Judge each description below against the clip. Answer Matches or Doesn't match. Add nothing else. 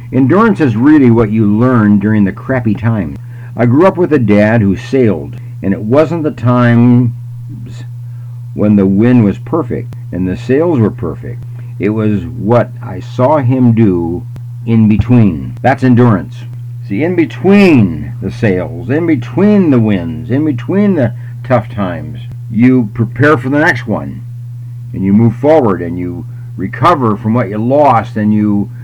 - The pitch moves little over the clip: Matches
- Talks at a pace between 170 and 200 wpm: Doesn't match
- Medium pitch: Doesn't match